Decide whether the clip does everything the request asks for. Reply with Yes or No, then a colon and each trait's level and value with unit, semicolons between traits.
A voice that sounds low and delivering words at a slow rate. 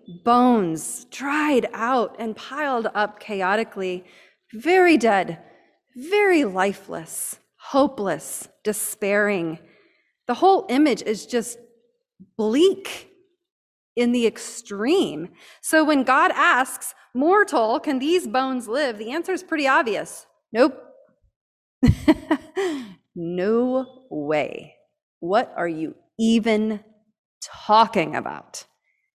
No: high, 245 Hz; slow, 95 wpm